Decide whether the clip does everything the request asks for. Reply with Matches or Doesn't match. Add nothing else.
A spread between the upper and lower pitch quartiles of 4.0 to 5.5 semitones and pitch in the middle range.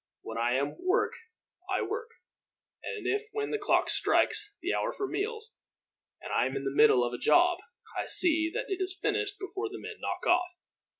Doesn't match